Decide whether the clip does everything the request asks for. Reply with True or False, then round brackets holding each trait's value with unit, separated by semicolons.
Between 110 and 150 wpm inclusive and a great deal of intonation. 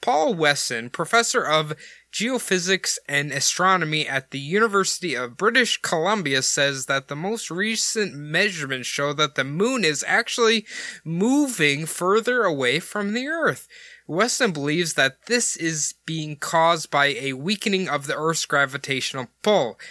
True (140 wpm; 6.9 semitones)